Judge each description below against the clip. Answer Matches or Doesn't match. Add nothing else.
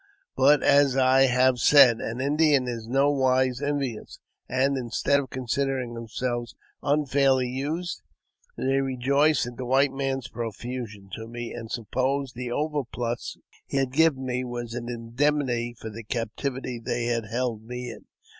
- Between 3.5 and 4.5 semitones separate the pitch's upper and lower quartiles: Doesn't match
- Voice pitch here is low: Matches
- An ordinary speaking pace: Matches